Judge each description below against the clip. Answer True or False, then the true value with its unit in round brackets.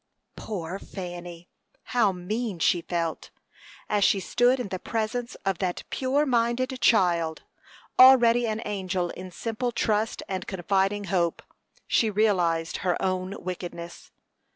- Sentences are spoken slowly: True (130 wpm)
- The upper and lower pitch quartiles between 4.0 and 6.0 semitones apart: True (4.4 semitones)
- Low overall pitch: False (195 Hz)